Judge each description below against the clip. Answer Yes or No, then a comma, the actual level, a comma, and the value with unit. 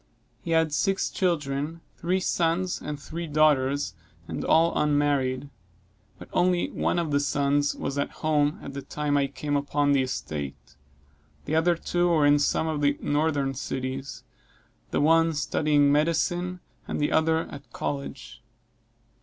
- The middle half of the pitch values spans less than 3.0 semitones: Yes, narrow, 2.4 semitones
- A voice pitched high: No, medium, 145 Hz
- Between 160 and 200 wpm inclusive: No, average, 150 wpm